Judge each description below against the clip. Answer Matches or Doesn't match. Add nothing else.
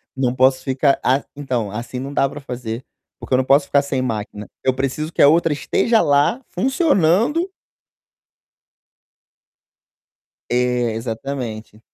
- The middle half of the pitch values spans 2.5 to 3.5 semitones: Matches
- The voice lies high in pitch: Doesn't match